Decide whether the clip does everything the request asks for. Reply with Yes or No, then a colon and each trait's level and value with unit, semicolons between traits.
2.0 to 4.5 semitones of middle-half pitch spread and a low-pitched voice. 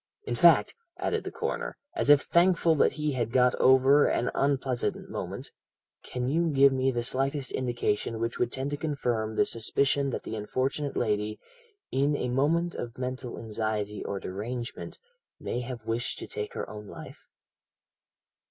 Yes: average, 3.4 semitones; low, 130 Hz